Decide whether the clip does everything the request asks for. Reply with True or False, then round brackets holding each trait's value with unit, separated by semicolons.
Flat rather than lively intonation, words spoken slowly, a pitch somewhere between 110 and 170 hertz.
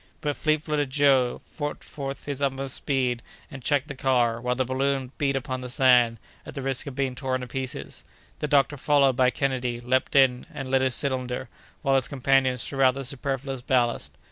False (1.6 semitones; 195 wpm; 135 Hz)